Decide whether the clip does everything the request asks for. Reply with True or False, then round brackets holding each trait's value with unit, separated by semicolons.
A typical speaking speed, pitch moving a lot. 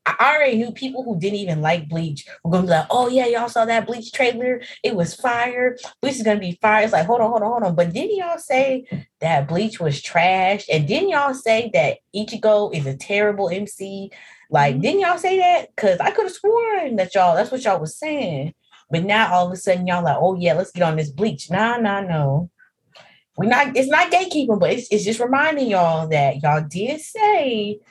False (225 wpm; 6.7 semitones)